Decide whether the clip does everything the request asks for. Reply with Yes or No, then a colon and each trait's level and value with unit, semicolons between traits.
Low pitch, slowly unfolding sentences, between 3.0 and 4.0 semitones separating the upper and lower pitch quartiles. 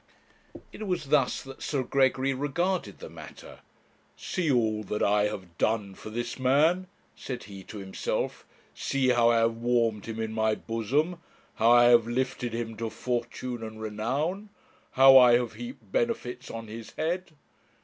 No: low, 120 Hz; average, 160 wpm; average, 3.5 semitones